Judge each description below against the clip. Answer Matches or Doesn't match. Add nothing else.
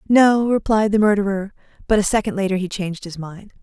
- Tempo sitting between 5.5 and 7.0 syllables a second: Matches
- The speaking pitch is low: Doesn't match